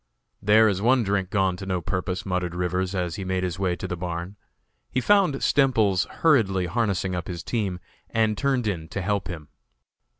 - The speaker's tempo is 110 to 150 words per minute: No, average, 190 wpm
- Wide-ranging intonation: No, average, 3.3 semitones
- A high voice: No, very low, 95 Hz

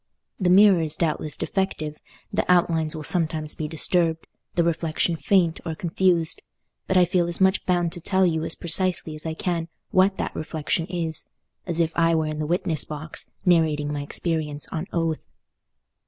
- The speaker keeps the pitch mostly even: Yes, narrow, 2.1 semitones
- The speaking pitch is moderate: Yes, medium, 165 Hz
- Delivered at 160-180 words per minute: Yes, average, 175 wpm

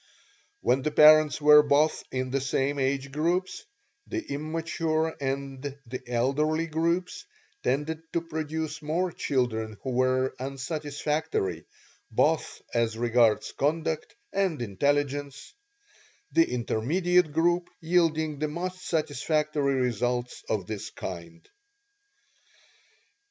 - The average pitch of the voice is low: No, medium, 150 Hz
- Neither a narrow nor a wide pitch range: Yes, average, 3.7 semitones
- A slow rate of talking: Yes, slow, 105 wpm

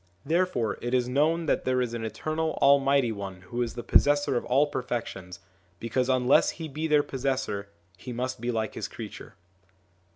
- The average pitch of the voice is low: Yes, low, 125 Hz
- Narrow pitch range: No, average, 3.8 semitones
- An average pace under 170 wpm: No, average, 175 wpm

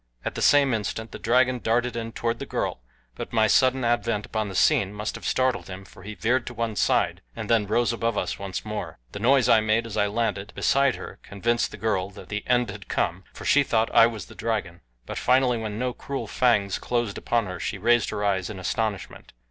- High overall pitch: No, low, 115 Hz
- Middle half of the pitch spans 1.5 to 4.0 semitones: Yes, average, 2.8 semitones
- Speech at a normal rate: No, fast, 230 wpm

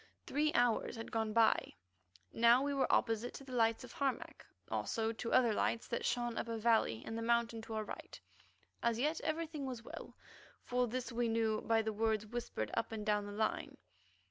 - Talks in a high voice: Yes, high, 230 Hz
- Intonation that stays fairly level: Yes, narrow, 1.9 semitones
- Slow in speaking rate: No, average, 195 wpm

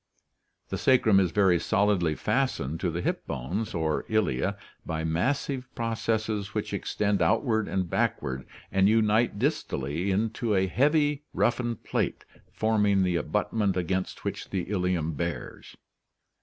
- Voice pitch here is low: Yes, low, 100 Hz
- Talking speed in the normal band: No, slow, 130 wpm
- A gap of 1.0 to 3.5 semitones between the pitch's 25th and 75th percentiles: No, average, 4.4 semitones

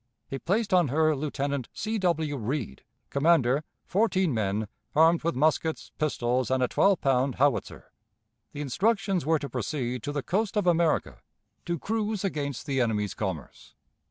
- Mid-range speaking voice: Yes, medium, 145 Hz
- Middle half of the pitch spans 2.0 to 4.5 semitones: No, wide, 5.4 semitones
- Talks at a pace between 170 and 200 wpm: No, average, 155 wpm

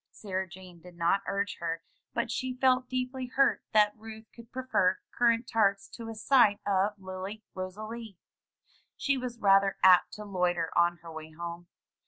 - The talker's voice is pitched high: Yes, high, 200 Hz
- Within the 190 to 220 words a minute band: No, average, 165 wpm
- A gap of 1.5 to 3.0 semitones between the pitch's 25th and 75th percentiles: No, average, 4.3 semitones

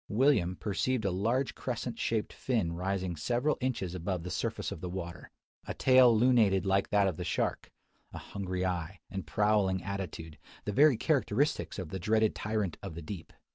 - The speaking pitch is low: Yes, low, 100 Hz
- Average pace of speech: Yes, average, 175 wpm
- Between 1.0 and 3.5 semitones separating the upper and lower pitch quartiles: No, average, 4.1 semitones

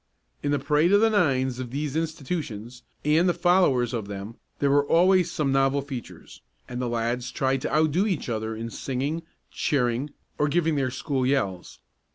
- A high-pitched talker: No, medium, 140 Hz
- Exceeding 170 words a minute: Yes, average, 180 wpm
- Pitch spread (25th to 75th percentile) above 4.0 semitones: Yes, average, 4.4 semitones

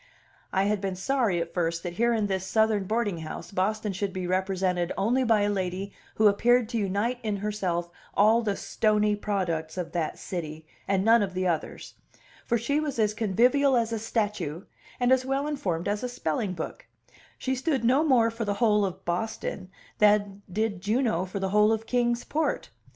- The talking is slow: No, average, 190 wpm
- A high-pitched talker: Yes, high, 205 Hz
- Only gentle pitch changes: No, average, 3.8 semitones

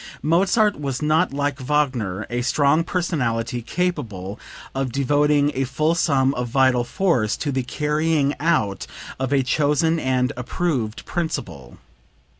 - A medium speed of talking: No, slow, 130 wpm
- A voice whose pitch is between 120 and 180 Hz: Yes, medium, 140 Hz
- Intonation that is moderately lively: Yes, average, 4.0 semitones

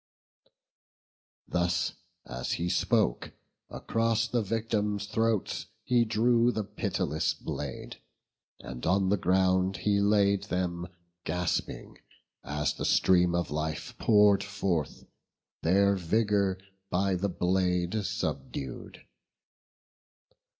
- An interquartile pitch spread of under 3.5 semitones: Yes, average, 3.0 semitones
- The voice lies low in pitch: Yes, very low, 95 Hz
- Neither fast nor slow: No, slow, 100 wpm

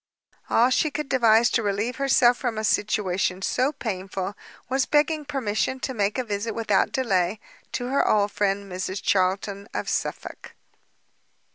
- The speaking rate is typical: Yes, average, 150 wpm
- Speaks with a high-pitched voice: Yes, high, 220 Hz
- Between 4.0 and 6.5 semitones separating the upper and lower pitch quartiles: Yes, average, 4.6 semitones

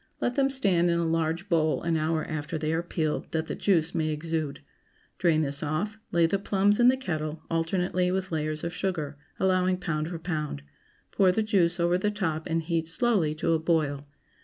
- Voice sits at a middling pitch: Yes, medium, 165 Hz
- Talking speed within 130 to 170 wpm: No, average, 200 wpm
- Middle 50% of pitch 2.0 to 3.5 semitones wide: Yes, average, 2.9 semitones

